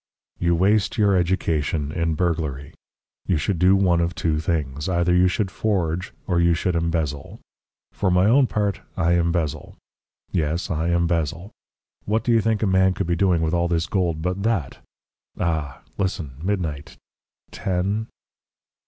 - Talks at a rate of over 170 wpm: No, average, 155 wpm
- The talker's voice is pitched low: Yes, very low, 85 Hz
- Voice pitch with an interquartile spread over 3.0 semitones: No, average, 2.7 semitones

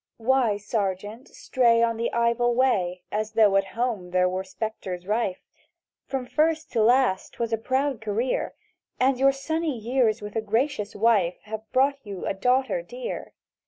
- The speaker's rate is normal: Yes, average, 160 wpm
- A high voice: Yes, high, 230 Hz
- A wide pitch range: No, average, 4.1 semitones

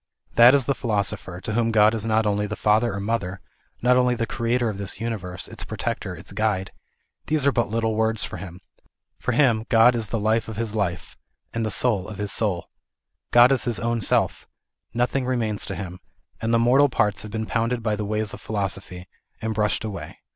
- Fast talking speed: Yes, fast, 210 wpm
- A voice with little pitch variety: Yes, narrow, 2.3 semitones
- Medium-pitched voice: No, low, 110 Hz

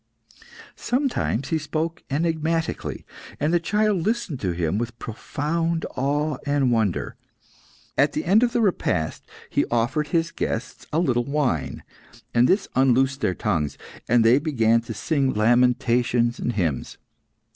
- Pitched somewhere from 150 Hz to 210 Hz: No, low, 135 Hz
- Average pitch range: No, wide, 5.8 semitones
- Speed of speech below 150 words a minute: Yes, average, 140 wpm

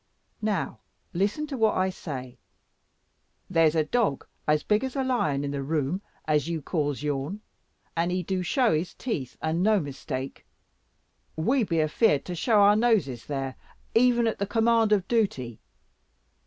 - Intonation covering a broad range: Yes, wide, 6.9 semitones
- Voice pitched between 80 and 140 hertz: No, medium, 180 Hz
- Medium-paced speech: Yes, average, 160 wpm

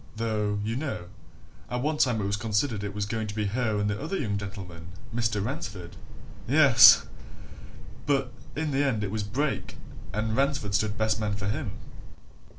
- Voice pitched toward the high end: No, low, 110 Hz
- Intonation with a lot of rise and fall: No, average, 4.0 semitones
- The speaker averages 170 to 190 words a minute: Yes, average, 175 wpm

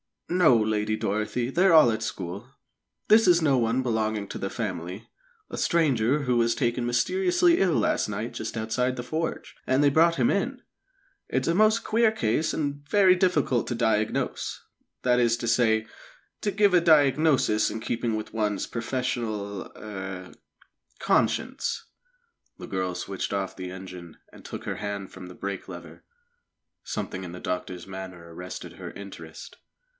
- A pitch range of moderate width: No, wide, 7.0 semitones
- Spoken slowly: No, average, 160 wpm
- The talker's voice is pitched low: Yes, low, 115 Hz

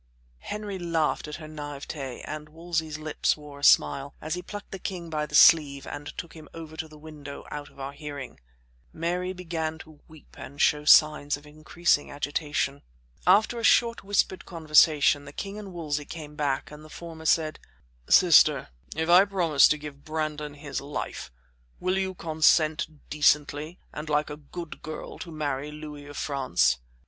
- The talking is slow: No, average, 175 wpm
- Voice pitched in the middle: Yes, medium, 155 Hz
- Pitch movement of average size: No, narrow, 2.3 semitones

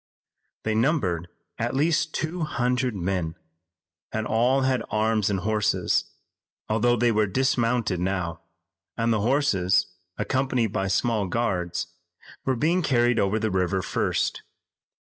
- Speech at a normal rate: No, slow, 125 wpm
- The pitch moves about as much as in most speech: Yes, average, 4.8 semitones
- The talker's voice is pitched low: Yes, low, 110 Hz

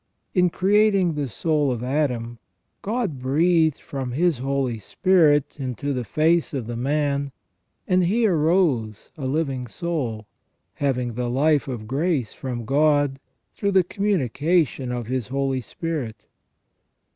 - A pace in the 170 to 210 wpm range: No, slow, 135 wpm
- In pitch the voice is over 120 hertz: Yes, medium, 140 Hz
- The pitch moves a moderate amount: Yes, average, 5.0 semitones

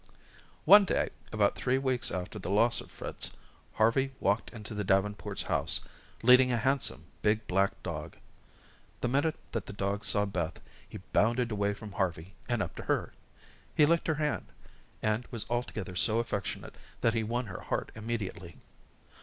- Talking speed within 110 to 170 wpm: Yes, average, 165 wpm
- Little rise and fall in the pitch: No, average, 3.7 semitones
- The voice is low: Yes, low, 110 Hz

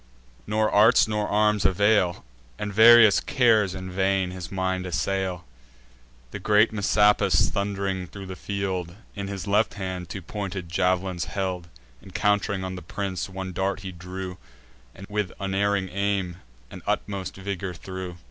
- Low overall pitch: Yes, very low, 95 Hz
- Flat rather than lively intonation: Yes, narrow, 1.7 semitones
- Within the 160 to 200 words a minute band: No, average, 145 wpm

